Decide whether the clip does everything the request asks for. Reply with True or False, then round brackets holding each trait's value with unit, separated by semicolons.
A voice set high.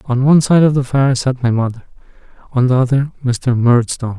False (130 Hz)